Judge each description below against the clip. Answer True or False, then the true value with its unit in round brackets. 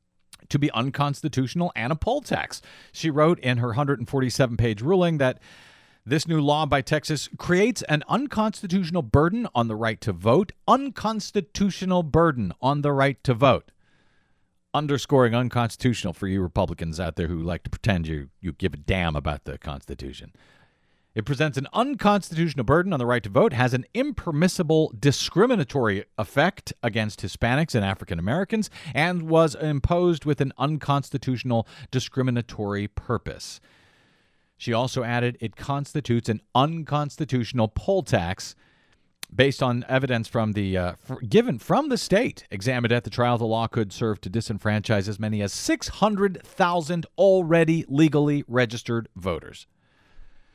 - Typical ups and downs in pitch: False (6.5 semitones)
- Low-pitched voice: True (130 Hz)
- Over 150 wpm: False (140 wpm)